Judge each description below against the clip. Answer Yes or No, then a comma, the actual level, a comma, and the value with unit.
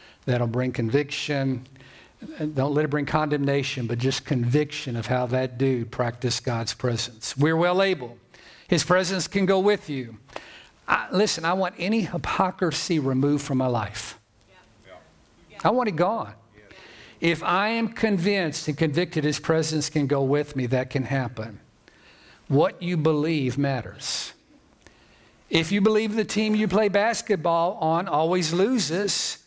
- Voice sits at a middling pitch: Yes, medium, 150 Hz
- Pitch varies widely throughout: Yes, wide, 5.8 semitones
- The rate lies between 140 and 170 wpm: Yes, average, 145 wpm